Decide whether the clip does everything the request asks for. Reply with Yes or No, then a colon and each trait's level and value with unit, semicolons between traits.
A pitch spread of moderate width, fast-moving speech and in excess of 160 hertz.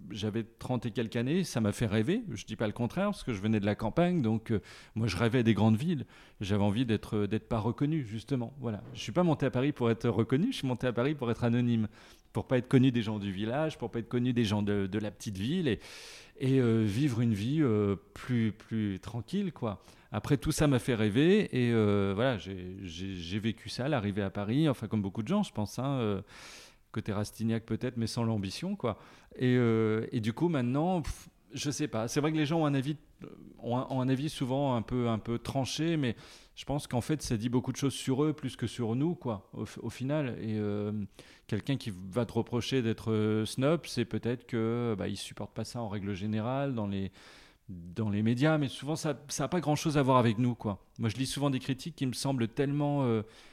No: average, 4.0 semitones; fast, 245 wpm; low, 120 Hz